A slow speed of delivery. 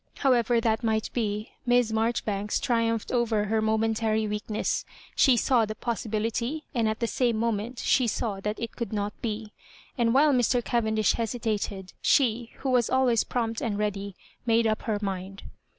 No: average, 165 wpm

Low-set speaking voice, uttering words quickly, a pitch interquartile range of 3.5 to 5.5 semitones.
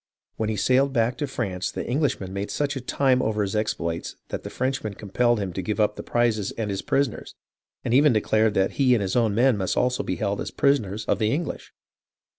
Yes: low, 110 Hz; fast, 230 wpm; average, 4.2 semitones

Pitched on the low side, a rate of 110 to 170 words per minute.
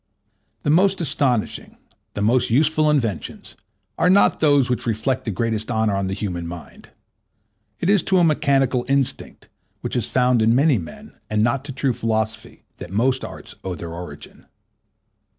Yes: low, 125 Hz; average, 165 wpm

